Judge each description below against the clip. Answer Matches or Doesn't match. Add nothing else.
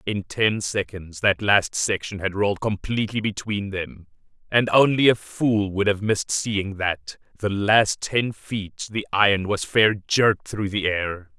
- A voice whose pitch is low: Matches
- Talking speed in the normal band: Matches